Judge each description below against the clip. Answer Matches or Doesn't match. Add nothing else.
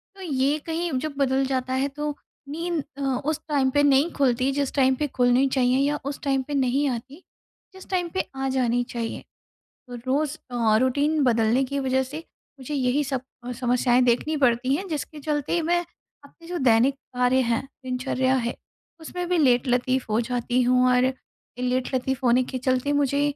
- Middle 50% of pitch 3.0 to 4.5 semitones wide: Doesn't match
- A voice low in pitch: Doesn't match